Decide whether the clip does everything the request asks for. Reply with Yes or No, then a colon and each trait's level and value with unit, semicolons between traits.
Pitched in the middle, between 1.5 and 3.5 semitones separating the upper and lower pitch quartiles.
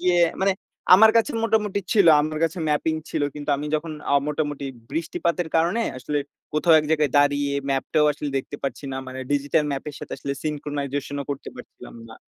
Yes: medium, 150 Hz; average, 2.9 semitones